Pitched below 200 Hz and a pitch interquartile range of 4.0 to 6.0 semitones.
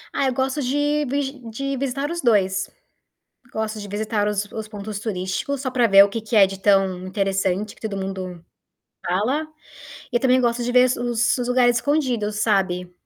No: high, 220 Hz; average, 4.6 semitones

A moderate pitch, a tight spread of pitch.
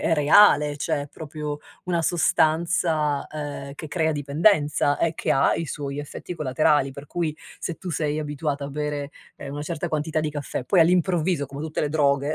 Yes: medium, 150 Hz; narrow, 2.0 semitones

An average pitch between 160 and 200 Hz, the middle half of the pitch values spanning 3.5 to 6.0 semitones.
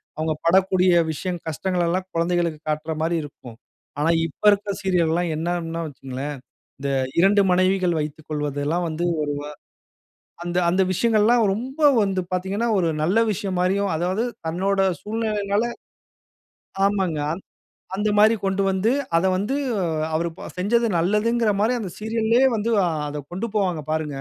Yes: medium, 185 Hz; average, 4.0 semitones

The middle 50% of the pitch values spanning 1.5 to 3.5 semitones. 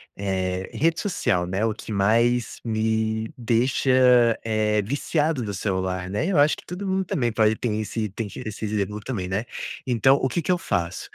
No: average, 4.1 semitones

